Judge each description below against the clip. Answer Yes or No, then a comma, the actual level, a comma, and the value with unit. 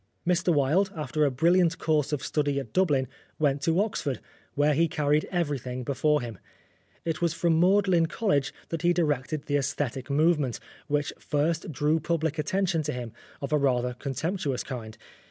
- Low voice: No, medium, 150 Hz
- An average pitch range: Yes, average, 3.3 semitones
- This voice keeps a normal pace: Yes, average, 165 wpm